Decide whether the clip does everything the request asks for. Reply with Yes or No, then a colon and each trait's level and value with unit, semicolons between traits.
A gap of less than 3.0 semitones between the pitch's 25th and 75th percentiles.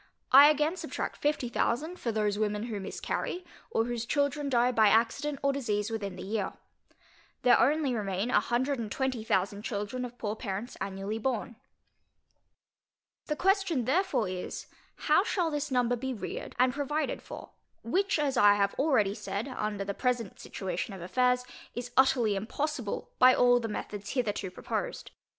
No: average, 4.9 semitones